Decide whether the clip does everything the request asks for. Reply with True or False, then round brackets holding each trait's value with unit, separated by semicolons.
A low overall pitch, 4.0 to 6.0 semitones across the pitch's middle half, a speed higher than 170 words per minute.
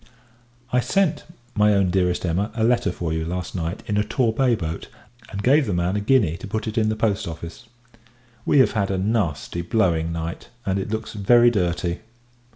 True (100 Hz; 4.4 semitones; 195 wpm)